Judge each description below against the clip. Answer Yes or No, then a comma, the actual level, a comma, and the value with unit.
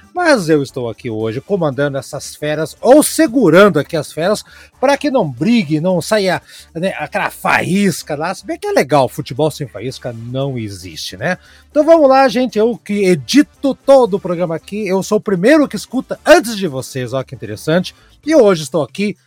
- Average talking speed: No, fast, 190 wpm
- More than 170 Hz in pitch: Yes, medium, 185 Hz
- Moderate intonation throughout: No, wide, 8.6 semitones